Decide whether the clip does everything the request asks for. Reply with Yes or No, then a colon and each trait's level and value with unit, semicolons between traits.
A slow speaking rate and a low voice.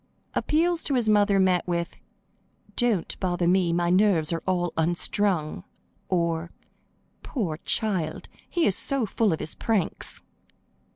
No: slow, 130 wpm; medium, 185 Hz